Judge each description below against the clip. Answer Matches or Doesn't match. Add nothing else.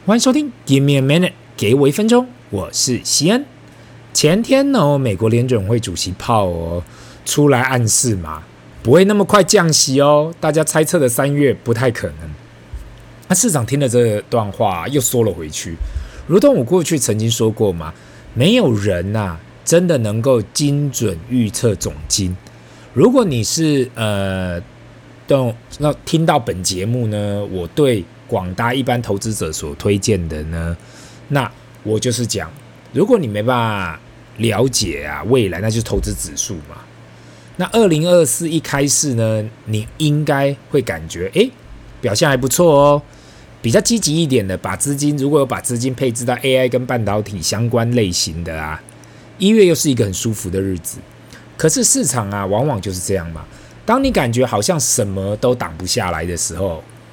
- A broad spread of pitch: Matches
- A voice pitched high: Doesn't match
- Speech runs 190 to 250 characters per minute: Doesn't match